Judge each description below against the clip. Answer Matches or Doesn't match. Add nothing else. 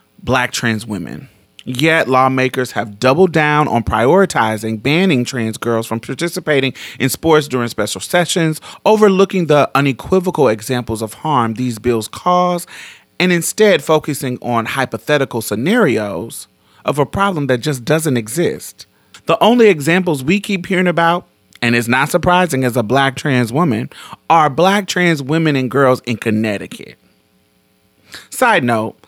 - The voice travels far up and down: Matches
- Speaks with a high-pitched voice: Doesn't match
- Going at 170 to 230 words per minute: Doesn't match